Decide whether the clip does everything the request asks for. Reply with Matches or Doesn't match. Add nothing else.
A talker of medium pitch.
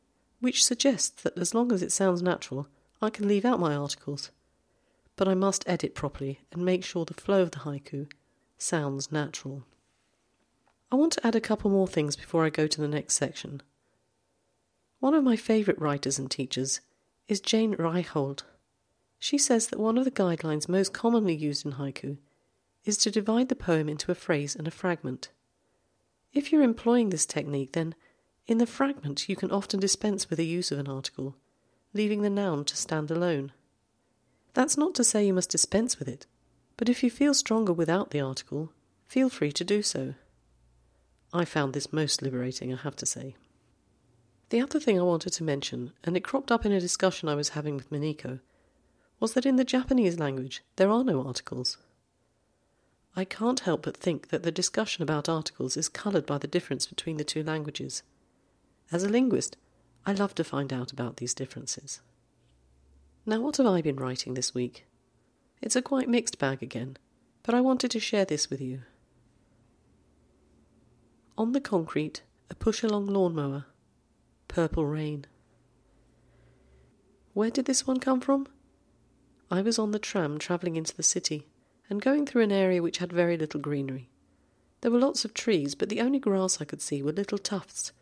Matches